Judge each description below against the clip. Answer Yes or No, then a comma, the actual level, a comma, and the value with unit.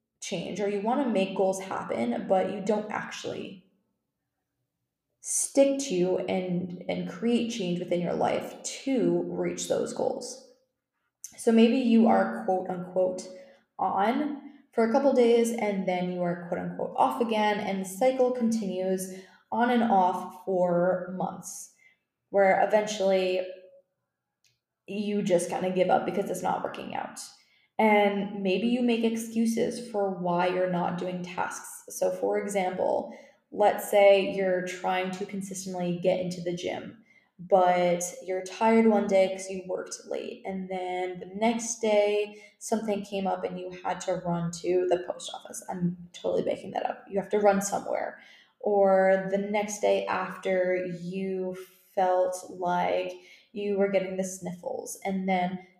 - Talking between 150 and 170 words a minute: Yes, average, 155 wpm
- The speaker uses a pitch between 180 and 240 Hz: Yes, high, 190 Hz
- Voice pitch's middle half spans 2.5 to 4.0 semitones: Yes, average, 2.8 semitones